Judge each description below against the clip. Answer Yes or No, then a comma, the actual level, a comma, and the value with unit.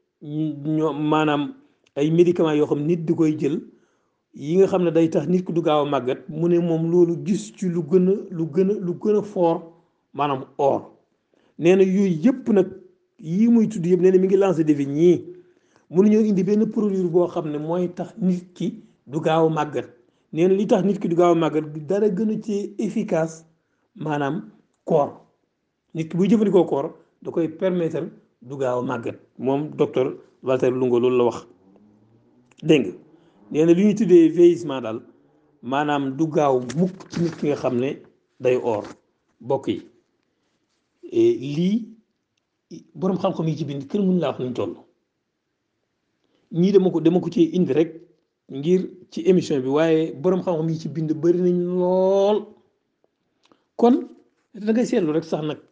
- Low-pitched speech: No, medium, 170 Hz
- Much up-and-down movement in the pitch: No, average, 4.0 semitones